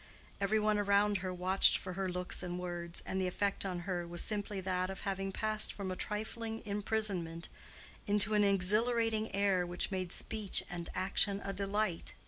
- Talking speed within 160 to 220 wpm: Yes, average, 175 wpm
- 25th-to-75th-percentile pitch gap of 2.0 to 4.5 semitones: Yes, narrow, 2.5 semitones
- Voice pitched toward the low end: No, high, 195 Hz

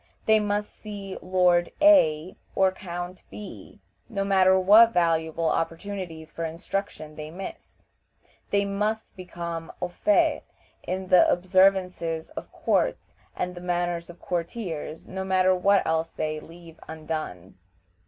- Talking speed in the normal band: No, slow, 130 wpm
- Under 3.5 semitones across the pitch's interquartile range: Yes, average, 3.0 semitones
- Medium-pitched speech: Yes, medium, 180 Hz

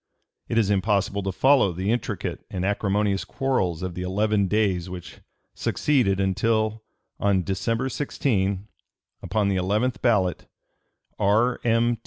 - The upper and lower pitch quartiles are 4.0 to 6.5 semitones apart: No, average, 3.2 semitones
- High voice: No, low, 100 Hz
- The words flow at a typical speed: No, slow, 130 wpm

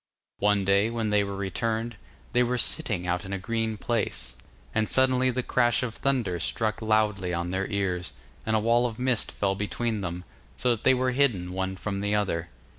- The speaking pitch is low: Yes, low, 105 Hz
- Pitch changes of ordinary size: Yes, average, 3.7 semitones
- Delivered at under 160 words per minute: No, average, 195 wpm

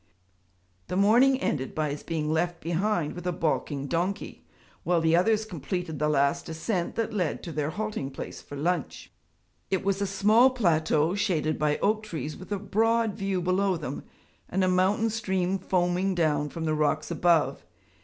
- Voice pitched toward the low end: No, medium, 180 Hz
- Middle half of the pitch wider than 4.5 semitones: No, average, 4.2 semitones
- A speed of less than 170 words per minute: No, average, 175 wpm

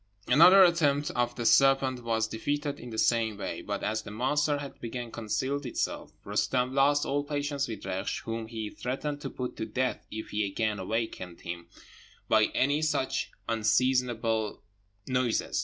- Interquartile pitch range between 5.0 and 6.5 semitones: No, average, 4.1 semitones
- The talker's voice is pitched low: Yes, low, 125 Hz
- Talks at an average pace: Yes, average, 160 wpm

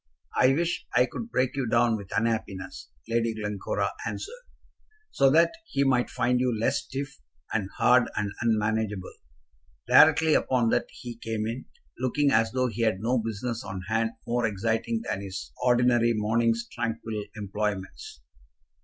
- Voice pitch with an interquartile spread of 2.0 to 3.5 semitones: Yes, narrow, 2.6 semitones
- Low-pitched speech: Yes, low, 115 Hz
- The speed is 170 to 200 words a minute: No, average, 150 wpm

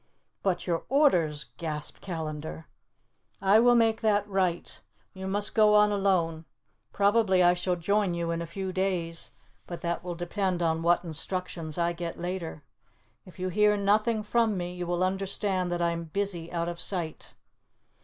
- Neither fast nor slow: Yes, average, 165 wpm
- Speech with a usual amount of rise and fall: Yes, average, 3.0 semitones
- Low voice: No, medium, 180 Hz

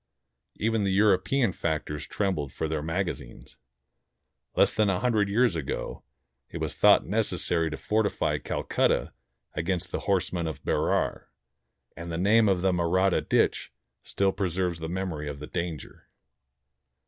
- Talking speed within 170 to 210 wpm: No, average, 145 wpm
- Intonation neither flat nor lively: Yes, average, 3.4 semitones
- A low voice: Yes, very low, 90 Hz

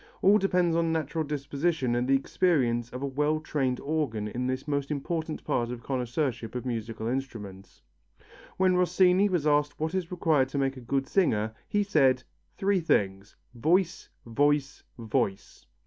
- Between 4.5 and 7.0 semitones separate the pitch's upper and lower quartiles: Yes, average, 5.0 semitones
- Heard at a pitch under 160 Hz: Yes, medium, 140 Hz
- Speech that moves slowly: No, average, 160 wpm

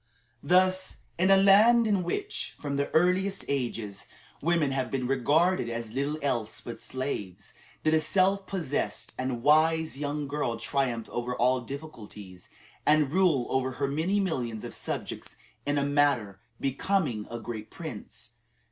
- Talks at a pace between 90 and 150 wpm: Yes, average, 145 wpm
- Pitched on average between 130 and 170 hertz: Yes, medium, 140 Hz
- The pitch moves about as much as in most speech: No, wide, 6.2 semitones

